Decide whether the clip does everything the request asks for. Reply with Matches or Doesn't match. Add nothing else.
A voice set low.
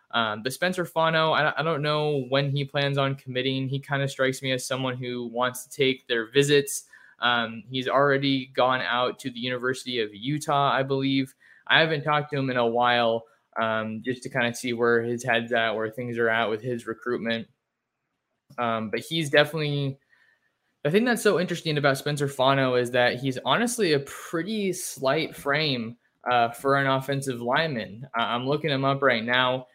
Matches